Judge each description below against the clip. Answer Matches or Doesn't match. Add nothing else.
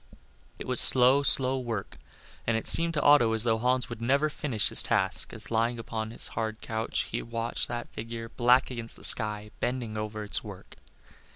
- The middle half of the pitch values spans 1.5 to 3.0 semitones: Matches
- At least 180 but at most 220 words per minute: Matches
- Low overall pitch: Matches